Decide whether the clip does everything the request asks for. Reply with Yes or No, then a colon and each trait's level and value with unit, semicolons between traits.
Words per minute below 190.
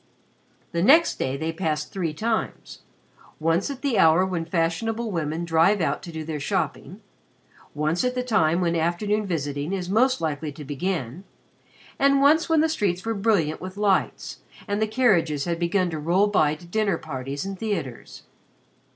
Yes: average, 170 wpm